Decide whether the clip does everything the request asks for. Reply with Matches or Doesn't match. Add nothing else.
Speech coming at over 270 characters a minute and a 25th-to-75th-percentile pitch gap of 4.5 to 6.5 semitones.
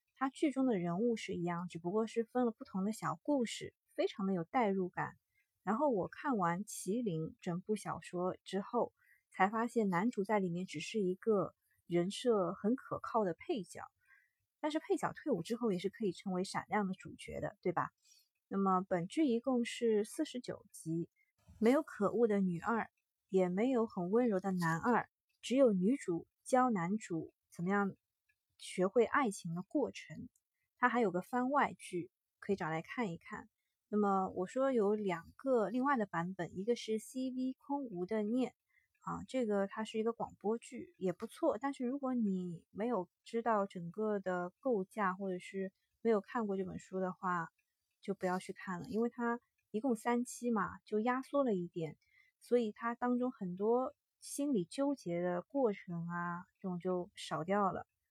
Doesn't match